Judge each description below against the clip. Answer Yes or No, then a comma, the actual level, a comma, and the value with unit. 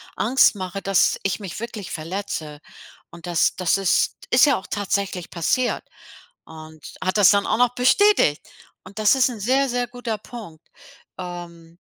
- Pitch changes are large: Yes, wide, 5.9 semitones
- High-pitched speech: Yes, high, 195 Hz